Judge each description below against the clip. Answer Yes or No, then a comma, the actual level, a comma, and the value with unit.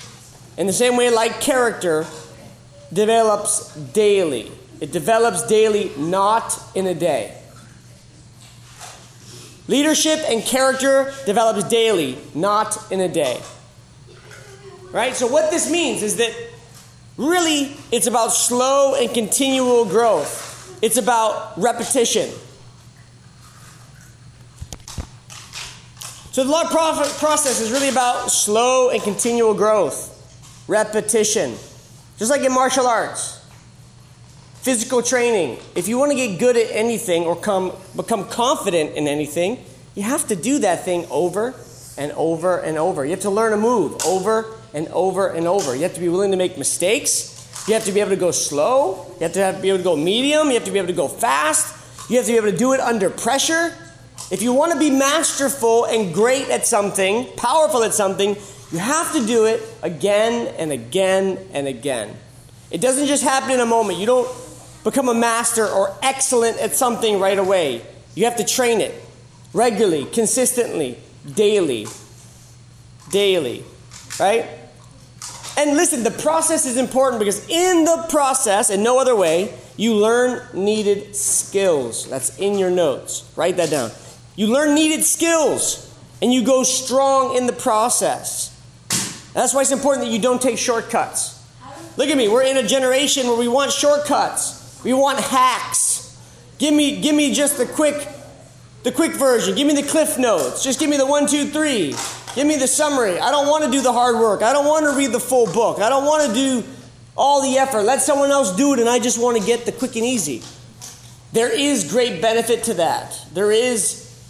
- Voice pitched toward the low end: No, high, 230 Hz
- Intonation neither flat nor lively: No, wide, 6.7 semitones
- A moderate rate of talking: Yes, average, 170 wpm